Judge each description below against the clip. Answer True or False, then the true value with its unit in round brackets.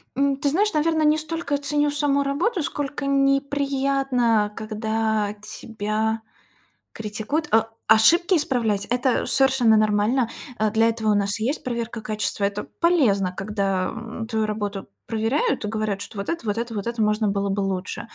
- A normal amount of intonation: True (4.7 semitones)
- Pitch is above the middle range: True (225 Hz)